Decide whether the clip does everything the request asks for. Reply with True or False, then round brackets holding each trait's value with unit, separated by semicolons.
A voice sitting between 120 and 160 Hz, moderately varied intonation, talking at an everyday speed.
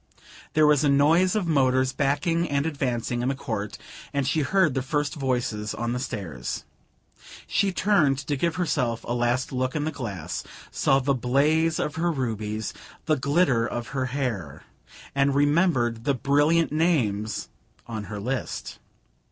True (135 Hz; 4.2 semitones; 160 wpm)